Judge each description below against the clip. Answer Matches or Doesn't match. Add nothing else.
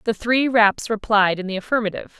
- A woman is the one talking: Matches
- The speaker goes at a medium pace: Matches